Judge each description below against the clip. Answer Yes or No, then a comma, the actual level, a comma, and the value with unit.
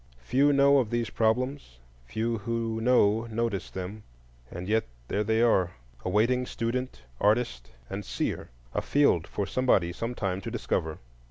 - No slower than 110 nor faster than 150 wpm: Yes, average, 140 wpm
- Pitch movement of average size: Yes, average, 4.4 semitones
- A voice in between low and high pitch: No, low, 110 Hz